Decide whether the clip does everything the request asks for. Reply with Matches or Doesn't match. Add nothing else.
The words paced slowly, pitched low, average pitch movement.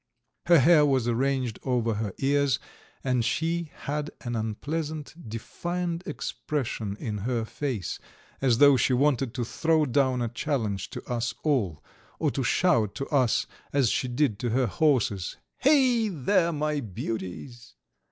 Doesn't match